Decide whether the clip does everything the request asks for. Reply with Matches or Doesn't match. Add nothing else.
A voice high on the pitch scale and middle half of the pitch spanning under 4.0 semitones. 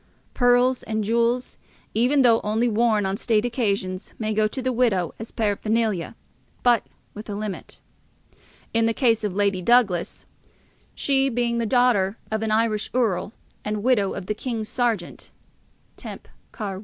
Matches